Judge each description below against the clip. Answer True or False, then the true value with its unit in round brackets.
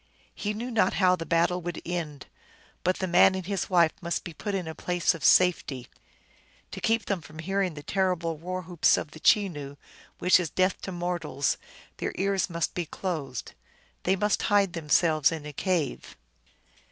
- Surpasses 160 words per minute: True (175 wpm)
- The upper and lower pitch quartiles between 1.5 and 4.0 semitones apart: True (2.8 semitones)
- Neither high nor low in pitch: True (175 Hz)